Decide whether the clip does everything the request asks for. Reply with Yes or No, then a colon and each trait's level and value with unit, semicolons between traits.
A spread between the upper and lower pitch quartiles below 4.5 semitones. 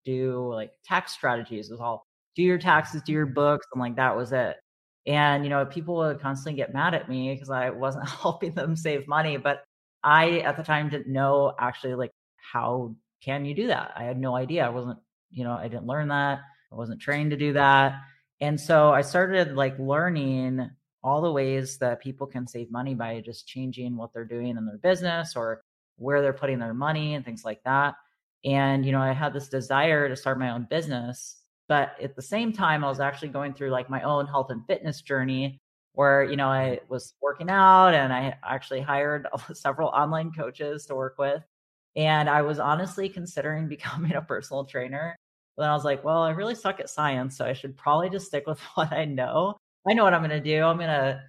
Yes: average, 2.8 semitones